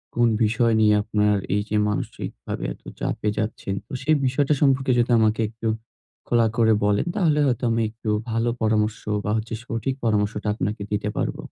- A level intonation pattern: Yes, narrow, 2.1 semitones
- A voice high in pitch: No, low, 110 Hz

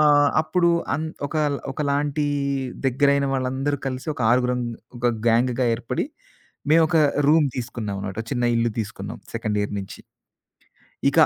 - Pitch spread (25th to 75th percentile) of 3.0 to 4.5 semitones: Yes, average, 3.7 semitones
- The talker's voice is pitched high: No, low, 130 Hz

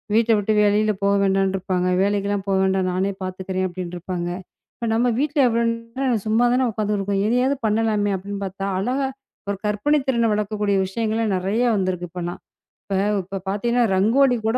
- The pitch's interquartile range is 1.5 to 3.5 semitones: Yes, average, 3.2 semitones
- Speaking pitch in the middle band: No, high, 205 Hz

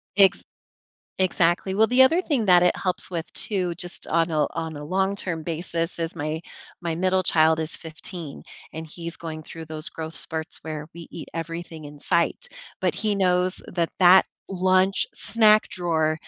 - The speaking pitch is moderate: Yes, medium, 170 Hz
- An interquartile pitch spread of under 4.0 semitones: Yes, average, 2.7 semitones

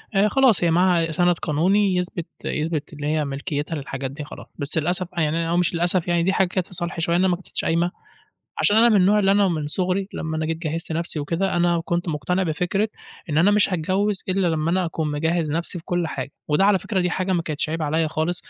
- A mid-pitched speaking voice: Yes, medium, 170 Hz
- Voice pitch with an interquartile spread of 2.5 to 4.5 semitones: Yes, average, 2.8 semitones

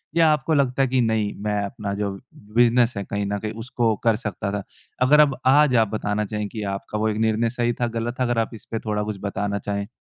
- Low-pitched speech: Yes, low, 110 Hz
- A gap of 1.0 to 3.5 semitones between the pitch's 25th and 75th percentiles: Yes, average, 2.9 semitones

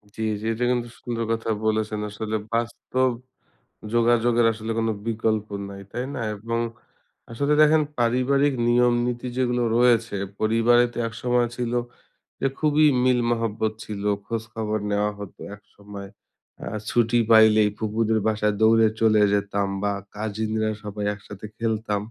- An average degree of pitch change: No, narrow, 2.0 semitones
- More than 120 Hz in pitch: No, low, 115 Hz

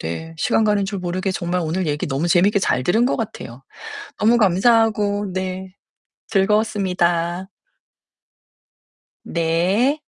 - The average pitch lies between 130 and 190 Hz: Yes, medium, 185 Hz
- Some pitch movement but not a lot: Yes, average, 3.4 semitones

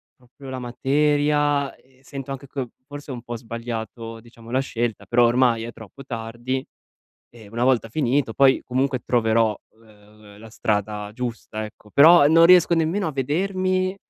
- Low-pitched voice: Yes, low, 125 Hz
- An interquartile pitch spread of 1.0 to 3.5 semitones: No, average, 3.9 semitones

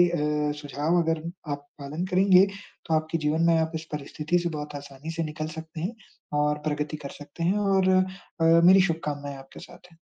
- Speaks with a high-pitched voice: No, medium, 160 Hz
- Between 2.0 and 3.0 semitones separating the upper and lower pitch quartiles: Yes, average, 2.7 semitones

